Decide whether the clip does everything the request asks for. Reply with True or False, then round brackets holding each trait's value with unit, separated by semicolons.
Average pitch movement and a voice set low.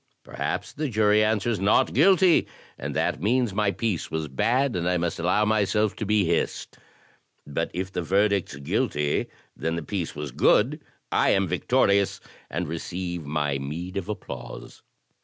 True (4.3 semitones; 95 Hz)